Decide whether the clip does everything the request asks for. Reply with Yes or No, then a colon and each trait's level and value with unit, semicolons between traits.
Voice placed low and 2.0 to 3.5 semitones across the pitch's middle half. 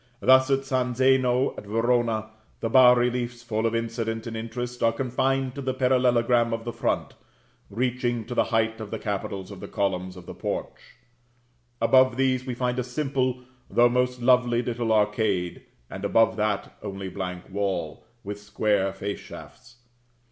Yes: low, 120 Hz; average, 3.1 semitones